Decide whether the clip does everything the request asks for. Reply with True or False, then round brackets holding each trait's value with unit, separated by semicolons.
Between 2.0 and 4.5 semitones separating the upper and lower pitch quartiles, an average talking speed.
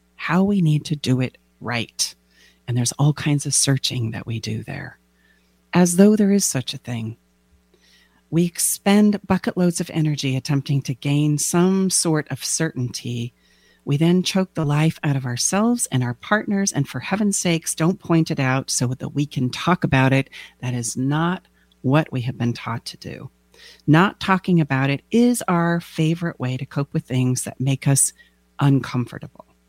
False (5.6 semitones; 180 wpm)